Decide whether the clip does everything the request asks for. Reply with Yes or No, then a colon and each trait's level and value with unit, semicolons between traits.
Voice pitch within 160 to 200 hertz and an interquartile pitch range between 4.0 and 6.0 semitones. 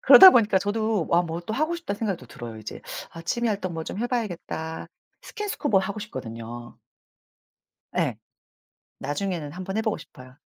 Yes: high, 190 Hz; wide, 5.5 semitones